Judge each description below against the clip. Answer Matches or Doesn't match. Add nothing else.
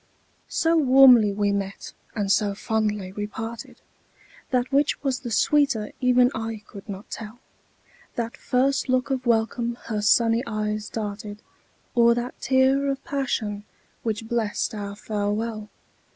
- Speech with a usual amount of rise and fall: Matches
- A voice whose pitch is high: Matches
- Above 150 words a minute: Doesn't match